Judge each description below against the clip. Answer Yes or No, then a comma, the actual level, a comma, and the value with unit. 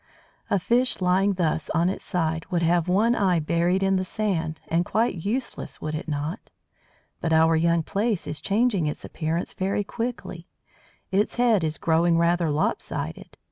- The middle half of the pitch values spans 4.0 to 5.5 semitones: No, average, 3.6 semitones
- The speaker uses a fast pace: No, average, 165 wpm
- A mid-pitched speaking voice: Yes, medium, 175 Hz